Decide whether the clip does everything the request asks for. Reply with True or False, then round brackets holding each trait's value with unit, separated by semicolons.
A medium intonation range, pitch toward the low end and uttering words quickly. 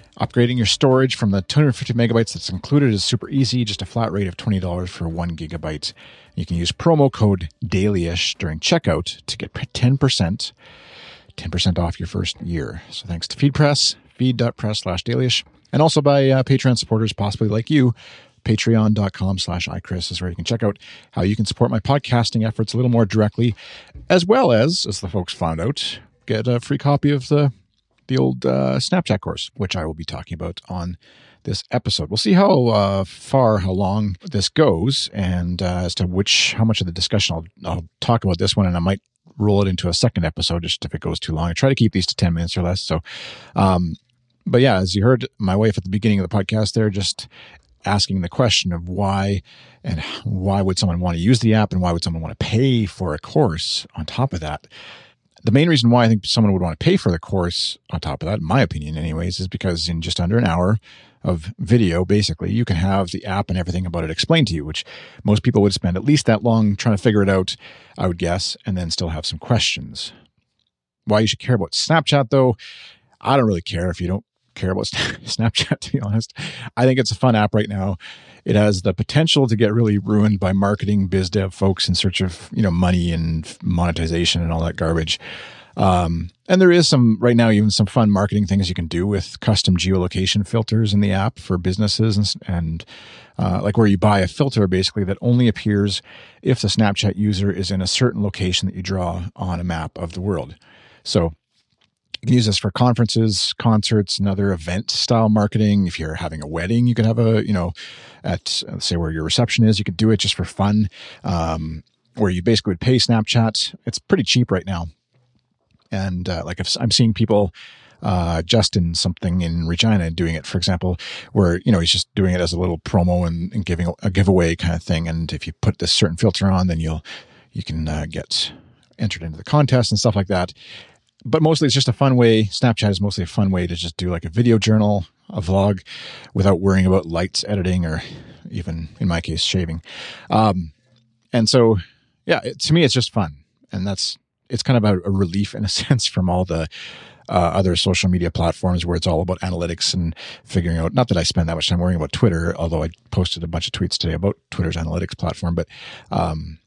True (4.2 semitones; 100 Hz; 220 wpm)